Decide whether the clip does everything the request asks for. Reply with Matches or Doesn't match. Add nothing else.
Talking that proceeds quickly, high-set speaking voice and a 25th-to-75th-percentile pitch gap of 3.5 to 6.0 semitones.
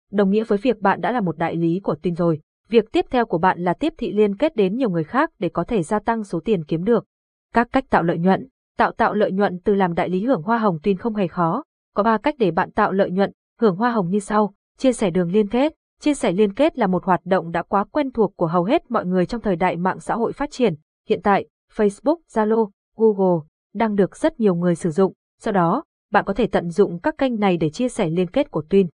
Matches